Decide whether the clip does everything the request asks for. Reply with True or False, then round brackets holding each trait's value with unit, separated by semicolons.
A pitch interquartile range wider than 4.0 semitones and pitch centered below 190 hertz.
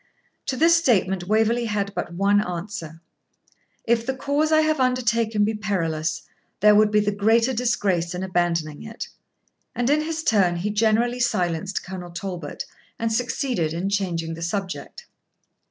False (5.0 semitones; 205 Hz)